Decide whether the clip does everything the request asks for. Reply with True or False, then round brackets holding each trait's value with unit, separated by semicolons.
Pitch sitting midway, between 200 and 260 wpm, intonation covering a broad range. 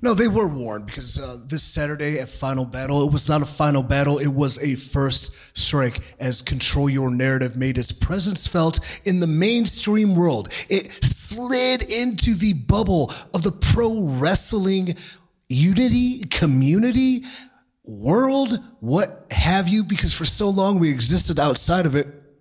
False (165 Hz; 155 wpm; 6.9 semitones)